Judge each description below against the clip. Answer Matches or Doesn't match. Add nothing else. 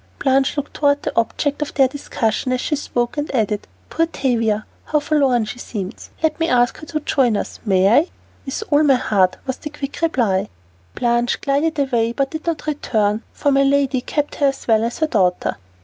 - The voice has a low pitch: Doesn't match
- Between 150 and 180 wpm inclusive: Doesn't match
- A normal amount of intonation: Matches